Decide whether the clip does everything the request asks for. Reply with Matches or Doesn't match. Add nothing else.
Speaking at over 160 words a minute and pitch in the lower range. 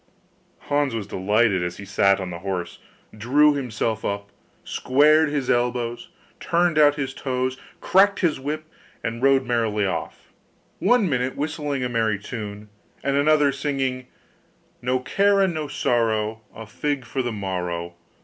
Doesn't match